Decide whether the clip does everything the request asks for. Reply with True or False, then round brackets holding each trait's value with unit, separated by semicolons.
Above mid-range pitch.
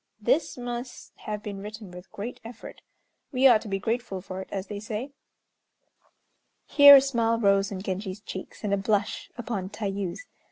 True (210 Hz)